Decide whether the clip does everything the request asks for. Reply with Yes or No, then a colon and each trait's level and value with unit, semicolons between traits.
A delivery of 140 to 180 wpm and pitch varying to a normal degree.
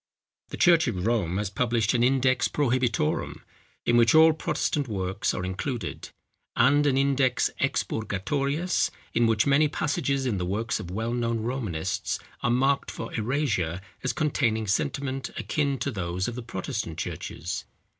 Yes: average, 150 wpm; average, 5.0 semitones